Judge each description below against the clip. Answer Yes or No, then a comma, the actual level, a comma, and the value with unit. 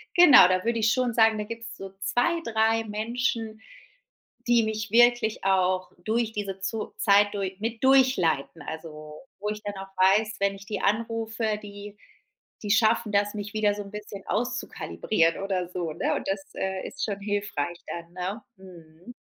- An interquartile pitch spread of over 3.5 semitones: No, average, 2.7 semitones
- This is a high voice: Yes, high, 210 Hz